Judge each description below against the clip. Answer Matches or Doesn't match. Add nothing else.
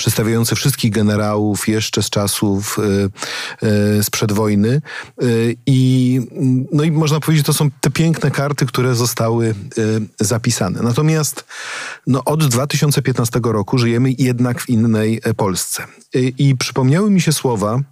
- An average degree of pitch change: Matches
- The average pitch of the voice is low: Matches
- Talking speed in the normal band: Matches